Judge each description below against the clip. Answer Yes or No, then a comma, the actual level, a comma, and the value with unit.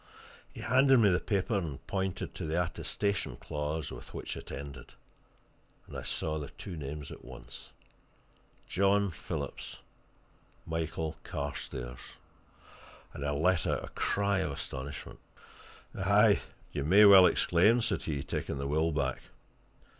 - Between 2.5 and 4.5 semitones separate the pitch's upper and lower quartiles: No, wide, 5.5 semitones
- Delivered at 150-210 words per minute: No, average, 140 wpm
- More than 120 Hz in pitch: No, very low, 80 Hz